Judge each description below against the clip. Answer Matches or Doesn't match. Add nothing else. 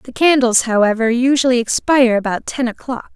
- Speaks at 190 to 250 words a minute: Doesn't match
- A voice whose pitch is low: Doesn't match